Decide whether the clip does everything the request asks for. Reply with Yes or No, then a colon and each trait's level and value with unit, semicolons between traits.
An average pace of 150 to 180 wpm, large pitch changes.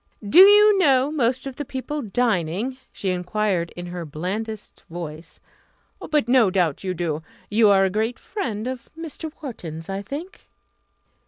Yes: average, 155 wpm; wide, 6.9 semitones